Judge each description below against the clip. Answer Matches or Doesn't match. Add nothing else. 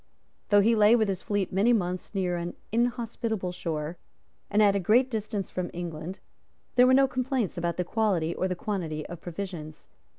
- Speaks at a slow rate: Doesn't match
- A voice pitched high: Matches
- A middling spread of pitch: Matches